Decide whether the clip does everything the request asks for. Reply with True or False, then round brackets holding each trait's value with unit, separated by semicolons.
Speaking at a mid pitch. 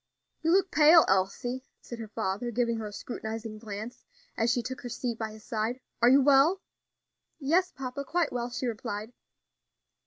False (240 Hz)